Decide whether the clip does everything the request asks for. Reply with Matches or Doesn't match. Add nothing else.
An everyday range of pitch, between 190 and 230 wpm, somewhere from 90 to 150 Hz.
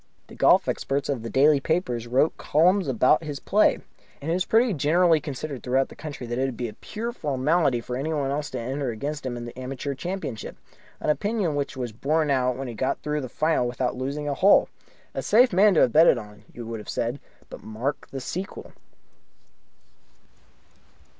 Matches